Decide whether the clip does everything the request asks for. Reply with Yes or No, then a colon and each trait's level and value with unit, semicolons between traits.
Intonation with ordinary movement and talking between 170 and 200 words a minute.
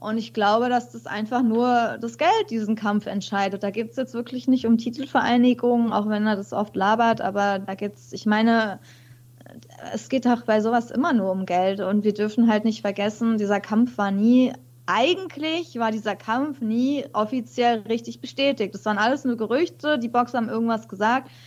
Yes: average, 3.0 semitones; average, 185 wpm